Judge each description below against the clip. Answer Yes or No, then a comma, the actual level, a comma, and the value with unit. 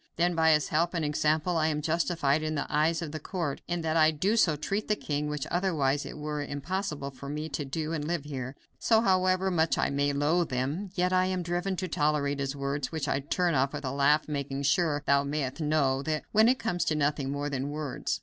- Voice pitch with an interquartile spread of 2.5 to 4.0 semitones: Yes, average, 3.3 semitones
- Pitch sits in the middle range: Yes, medium, 155 Hz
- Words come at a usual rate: No, fast, 225 wpm